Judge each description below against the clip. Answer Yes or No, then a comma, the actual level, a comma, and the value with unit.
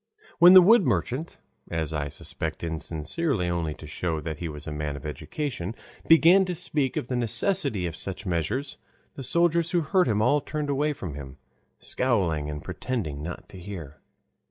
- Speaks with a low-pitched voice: Yes, low, 100 Hz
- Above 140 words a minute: Yes, average, 180 wpm